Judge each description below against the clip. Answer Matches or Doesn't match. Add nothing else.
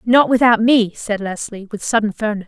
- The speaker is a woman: Matches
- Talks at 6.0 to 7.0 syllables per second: Doesn't match